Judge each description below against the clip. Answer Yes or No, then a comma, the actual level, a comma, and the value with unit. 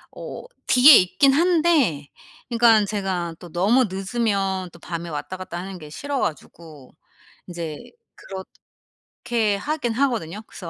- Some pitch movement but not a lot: No, wide, 6.0 semitones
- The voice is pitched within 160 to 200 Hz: Yes, high, 195 Hz